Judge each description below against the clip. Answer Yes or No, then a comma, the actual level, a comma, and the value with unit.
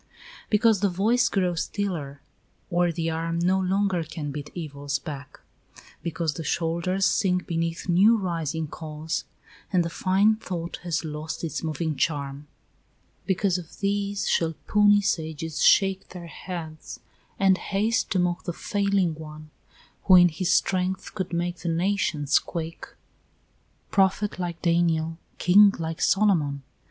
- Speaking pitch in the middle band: Yes, medium, 175 Hz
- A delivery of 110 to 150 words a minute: Yes, average, 140 wpm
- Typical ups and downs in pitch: Yes, average, 3.2 semitones